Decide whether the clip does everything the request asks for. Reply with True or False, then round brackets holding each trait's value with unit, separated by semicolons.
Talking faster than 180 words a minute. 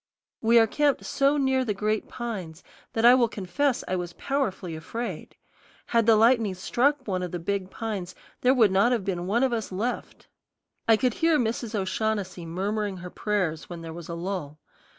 True (190 wpm)